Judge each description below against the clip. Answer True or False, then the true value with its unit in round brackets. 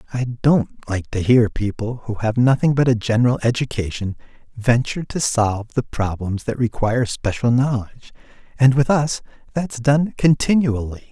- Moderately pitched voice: False (120 Hz)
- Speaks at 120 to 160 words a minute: True (150 wpm)